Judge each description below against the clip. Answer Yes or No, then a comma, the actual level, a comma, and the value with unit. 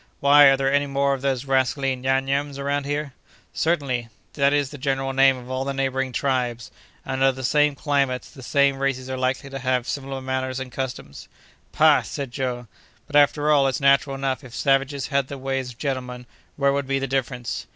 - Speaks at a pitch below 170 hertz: Yes, low, 135 Hz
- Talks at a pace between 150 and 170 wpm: No, fast, 205 wpm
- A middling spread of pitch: No, narrow, 1.2 semitones